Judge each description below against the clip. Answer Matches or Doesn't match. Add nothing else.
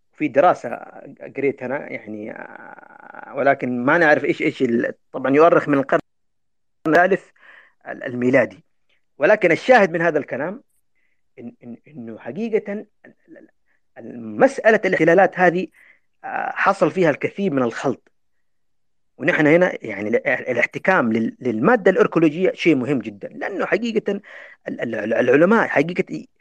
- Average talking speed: Doesn't match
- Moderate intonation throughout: Doesn't match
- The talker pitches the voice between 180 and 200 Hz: Matches